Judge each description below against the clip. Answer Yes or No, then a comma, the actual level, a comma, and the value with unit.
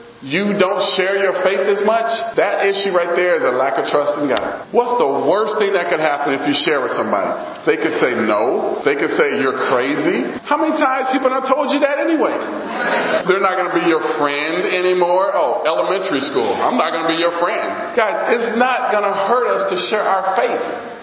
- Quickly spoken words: Yes, fast, 220 wpm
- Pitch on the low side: No, high, 205 Hz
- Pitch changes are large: Yes, wide, 6.5 semitones